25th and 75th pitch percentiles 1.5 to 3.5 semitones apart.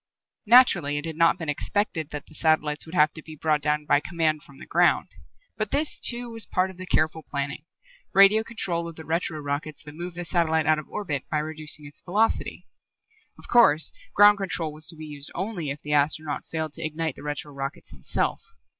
Yes: average, 2.9 semitones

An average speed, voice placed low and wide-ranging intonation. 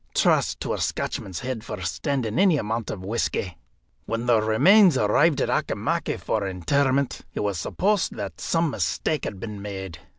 Yes: average, 165 wpm; low, 115 Hz; wide, 5.9 semitones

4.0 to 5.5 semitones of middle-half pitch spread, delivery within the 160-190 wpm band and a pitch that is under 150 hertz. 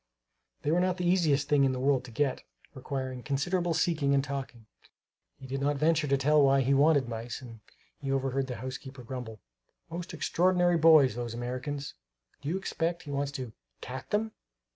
No: average, 3.5 semitones; average, 185 wpm; medium, 140 Hz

